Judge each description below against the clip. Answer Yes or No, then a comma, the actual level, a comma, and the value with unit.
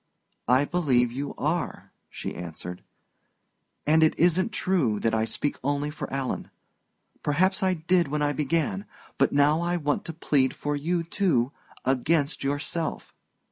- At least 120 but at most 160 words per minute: Yes, average, 145 wpm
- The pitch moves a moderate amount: Yes, average, 3.9 semitones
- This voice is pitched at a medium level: Yes, medium, 150 Hz